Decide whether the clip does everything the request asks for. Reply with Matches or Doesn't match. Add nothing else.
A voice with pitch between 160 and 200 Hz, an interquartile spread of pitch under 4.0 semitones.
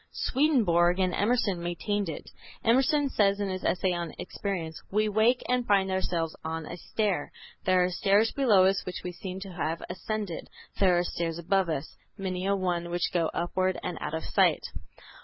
Matches